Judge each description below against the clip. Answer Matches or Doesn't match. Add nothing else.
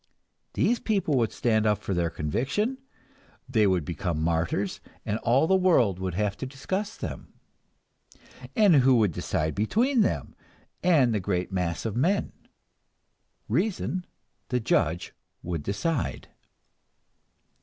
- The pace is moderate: Doesn't match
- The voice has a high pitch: Doesn't match